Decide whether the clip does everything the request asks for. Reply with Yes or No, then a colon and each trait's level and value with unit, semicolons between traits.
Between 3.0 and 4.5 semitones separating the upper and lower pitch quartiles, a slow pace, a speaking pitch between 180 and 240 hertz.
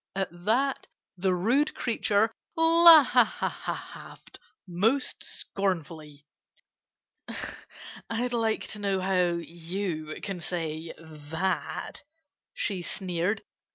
No: average, 5.1 semitones; slow, 85 wpm; high, 190 Hz